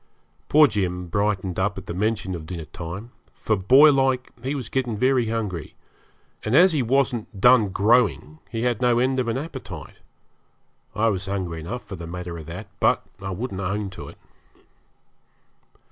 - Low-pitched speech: Yes, low, 105 Hz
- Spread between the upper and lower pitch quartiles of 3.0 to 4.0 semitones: No, average, 5.2 semitones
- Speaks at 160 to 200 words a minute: Yes, average, 170 wpm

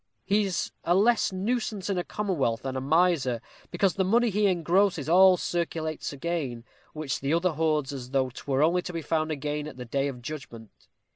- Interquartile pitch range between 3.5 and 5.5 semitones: Yes, average, 5.2 semitones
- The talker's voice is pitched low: No, medium, 160 Hz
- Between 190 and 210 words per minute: Yes, average, 195 wpm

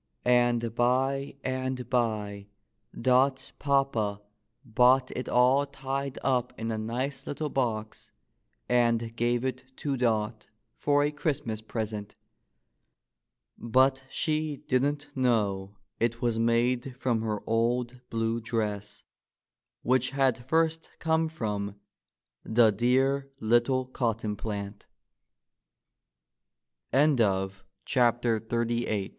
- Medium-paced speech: No, slow, 95 wpm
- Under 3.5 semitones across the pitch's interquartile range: Yes, average, 2.9 semitones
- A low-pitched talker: Yes, low, 120 Hz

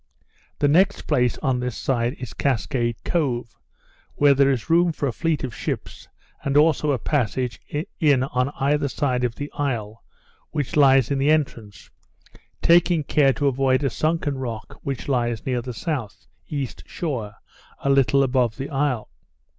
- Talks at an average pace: Yes, average, 160 wpm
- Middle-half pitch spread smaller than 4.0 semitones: Yes, average, 2.9 semitones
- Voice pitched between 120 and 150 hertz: Yes, low, 135 Hz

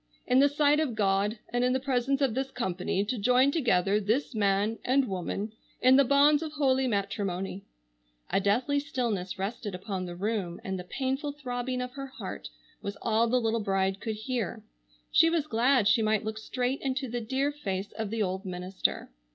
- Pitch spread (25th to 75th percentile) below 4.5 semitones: No, average, 5.1 semitones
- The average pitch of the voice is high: Yes, high, 225 Hz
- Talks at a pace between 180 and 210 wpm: Yes, average, 185 wpm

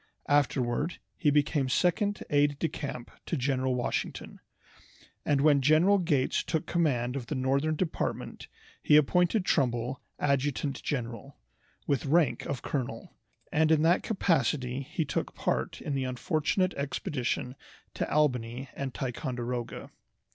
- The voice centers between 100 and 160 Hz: Yes, medium, 140 Hz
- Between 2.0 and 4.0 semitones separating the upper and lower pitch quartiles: Yes, average, 3.5 semitones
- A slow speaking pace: Yes, slow, 130 wpm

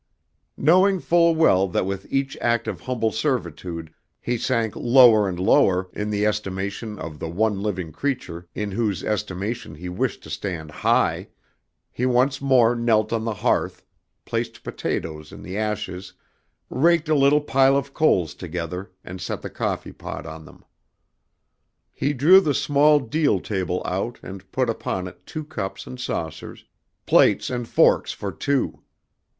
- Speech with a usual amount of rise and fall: No, wide, 6.3 semitones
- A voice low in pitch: Yes, low, 110 Hz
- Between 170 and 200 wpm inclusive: No, average, 155 wpm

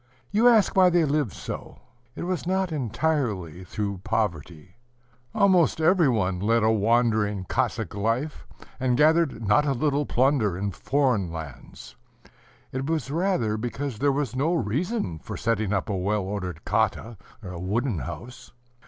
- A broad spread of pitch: Yes, wide, 6.7 semitones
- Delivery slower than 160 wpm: Yes, average, 145 wpm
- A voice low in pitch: Yes, low, 115 Hz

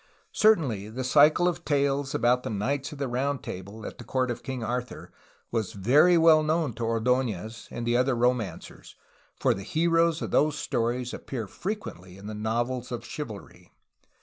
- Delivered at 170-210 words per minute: Yes, average, 175 wpm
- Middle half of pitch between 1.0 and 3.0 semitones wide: No, average, 4.5 semitones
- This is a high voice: No, low, 125 Hz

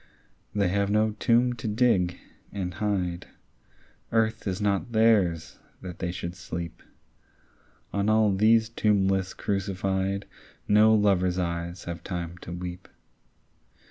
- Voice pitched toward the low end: Yes, very low, 95 Hz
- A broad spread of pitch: No, average, 3.2 semitones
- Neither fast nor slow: No, slow, 120 wpm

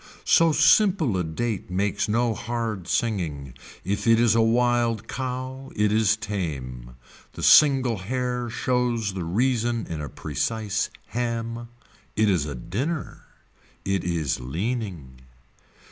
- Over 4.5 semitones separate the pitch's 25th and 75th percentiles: Yes, average, 5.2 semitones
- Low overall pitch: Yes, low, 110 Hz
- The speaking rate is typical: No, slow, 130 wpm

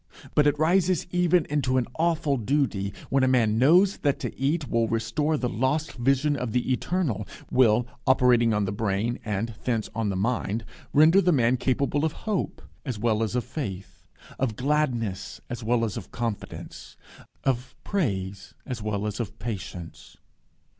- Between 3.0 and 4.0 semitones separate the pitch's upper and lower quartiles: No, average, 5.1 semitones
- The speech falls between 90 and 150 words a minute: No, average, 165 wpm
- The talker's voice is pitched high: No, low, 125 Hz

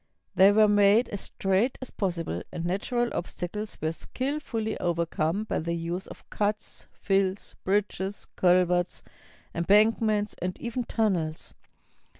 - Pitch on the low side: No, high, 195 Hz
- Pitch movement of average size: Yes, average, 3.5 semitones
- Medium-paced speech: No, slow, 125 wpm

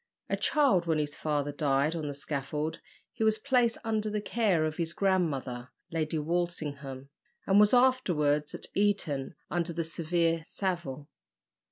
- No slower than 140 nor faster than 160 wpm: Yes, average, 150 wpm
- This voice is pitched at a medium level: Yes, medium, 165 Hz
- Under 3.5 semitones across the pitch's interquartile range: No, average, 5.1 semitones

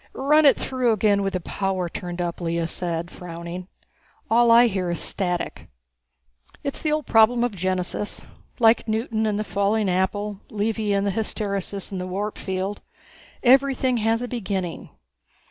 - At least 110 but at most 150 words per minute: No, average, 160 wpm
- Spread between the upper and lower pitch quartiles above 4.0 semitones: No, average, 3.7 semitones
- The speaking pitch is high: Yes, high, 205 Hz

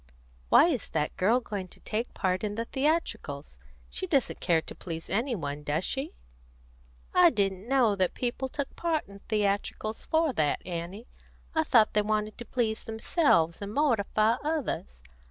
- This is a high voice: Yes, high, 215 Hz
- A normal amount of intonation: No, wide, 6.1 semitones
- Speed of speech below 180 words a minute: Yes, average, 165 wpm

